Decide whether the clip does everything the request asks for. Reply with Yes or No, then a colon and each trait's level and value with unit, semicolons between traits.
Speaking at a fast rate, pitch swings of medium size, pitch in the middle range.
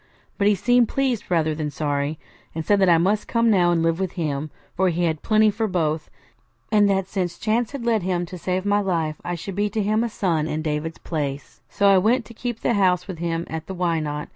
Yes: fast, 240 wpm; average, 4.4 semitones; medium, 180 Hz